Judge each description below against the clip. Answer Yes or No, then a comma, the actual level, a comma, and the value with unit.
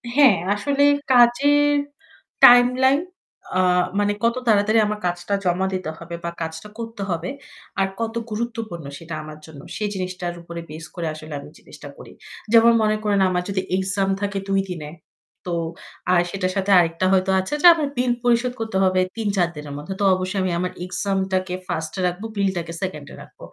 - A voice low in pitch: No, high, 190 Hz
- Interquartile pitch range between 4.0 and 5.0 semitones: Yes, average, 4.3 semitones